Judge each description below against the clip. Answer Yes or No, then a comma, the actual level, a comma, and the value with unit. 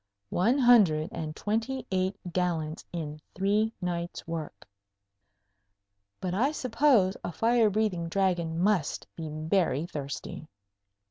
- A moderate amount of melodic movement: Yes, average, 4.8 semitones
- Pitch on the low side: No, medium, 180 Hz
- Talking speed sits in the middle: No, slow, 115 wpm